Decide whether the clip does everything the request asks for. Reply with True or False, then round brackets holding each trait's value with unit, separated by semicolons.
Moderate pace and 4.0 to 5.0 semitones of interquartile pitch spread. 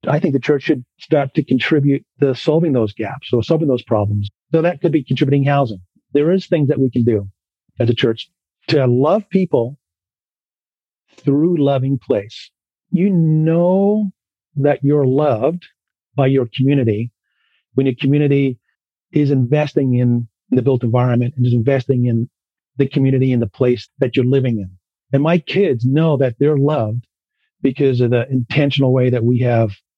False (165 wpm; 3.5 semitones)